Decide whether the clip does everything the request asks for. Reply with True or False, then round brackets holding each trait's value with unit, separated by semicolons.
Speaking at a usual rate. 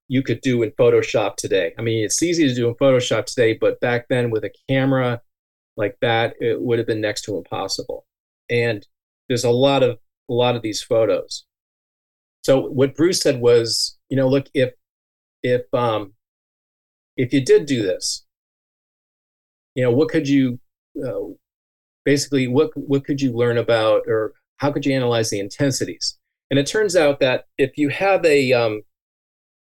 True (175 wpm)